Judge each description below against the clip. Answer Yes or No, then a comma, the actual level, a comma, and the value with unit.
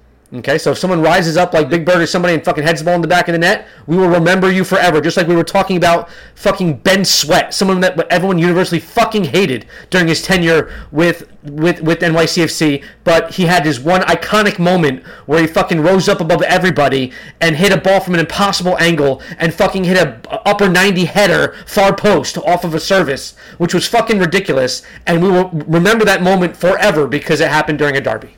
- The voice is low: No, medium, 175 Hz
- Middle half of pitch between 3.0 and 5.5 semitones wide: No, narrow, 2.6 semitones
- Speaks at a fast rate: Yes, fast, 215 wpm